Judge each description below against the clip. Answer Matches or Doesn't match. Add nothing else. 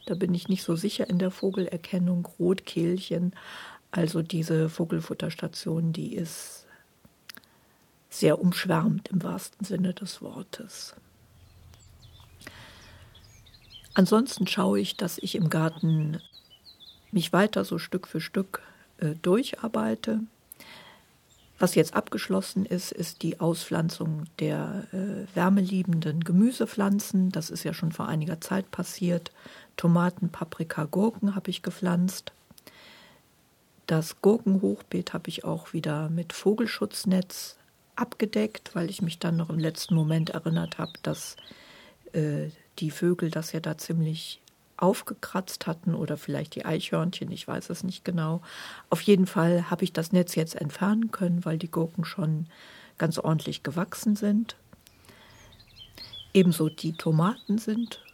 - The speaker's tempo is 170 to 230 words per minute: Doesn't match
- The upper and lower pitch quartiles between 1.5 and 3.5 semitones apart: Matches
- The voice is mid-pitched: Matches